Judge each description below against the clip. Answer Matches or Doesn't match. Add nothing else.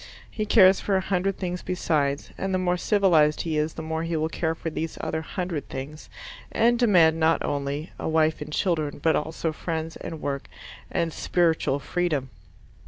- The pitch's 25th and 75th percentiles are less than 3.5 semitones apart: Matches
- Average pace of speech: Matches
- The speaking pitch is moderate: Matches